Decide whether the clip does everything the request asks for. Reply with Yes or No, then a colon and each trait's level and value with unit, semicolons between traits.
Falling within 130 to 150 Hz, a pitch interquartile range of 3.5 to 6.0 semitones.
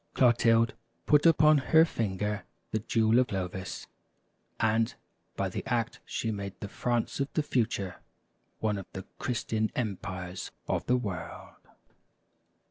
No: low, 110 Hz; average, 3.9 semitones